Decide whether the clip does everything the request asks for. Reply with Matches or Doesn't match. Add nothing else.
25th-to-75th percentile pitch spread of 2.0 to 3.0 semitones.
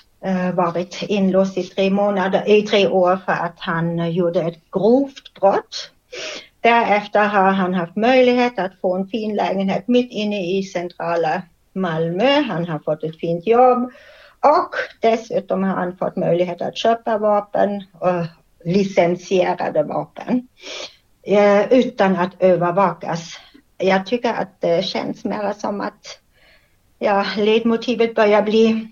Doesn't match